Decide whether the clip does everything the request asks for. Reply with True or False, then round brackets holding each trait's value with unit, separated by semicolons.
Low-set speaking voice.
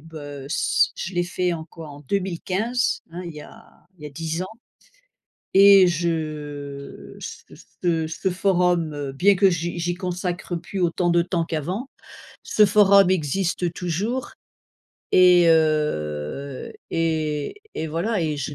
False (170 Hz)